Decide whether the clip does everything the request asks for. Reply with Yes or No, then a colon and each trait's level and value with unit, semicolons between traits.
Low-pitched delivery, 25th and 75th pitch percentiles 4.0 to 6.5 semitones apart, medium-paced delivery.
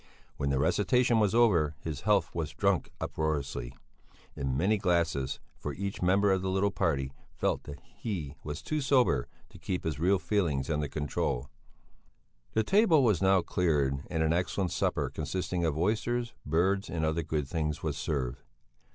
Yes: very low, 85 Hz; average, 5.1 semitones; average, 165 wpm